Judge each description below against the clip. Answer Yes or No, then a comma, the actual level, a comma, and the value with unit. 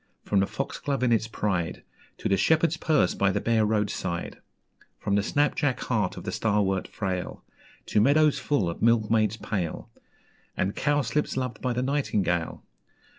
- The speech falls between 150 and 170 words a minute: Yes, average, 165 wpm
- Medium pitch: No, low, 110 Hz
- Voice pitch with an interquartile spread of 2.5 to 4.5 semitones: No, average, 5.1 semitones